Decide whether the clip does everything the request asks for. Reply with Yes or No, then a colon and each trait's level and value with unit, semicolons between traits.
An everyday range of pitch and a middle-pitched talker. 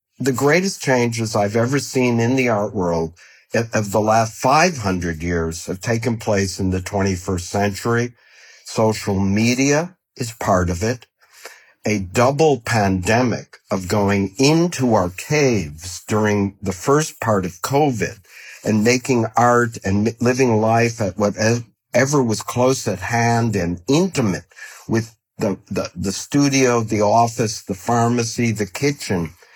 No: average, 3.7 semitones; low, 110 Hz